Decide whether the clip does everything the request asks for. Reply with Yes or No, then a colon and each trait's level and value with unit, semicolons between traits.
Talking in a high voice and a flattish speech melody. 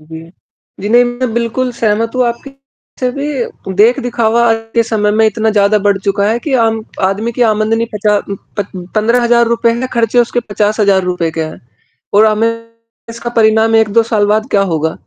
Yes: high, 225 Hz; narrow, 2.3 semitones